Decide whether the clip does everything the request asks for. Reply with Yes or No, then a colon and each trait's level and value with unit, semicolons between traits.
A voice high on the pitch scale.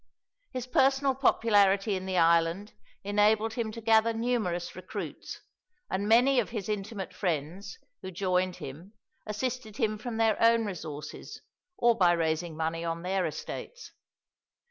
Yes: high, 205 Hz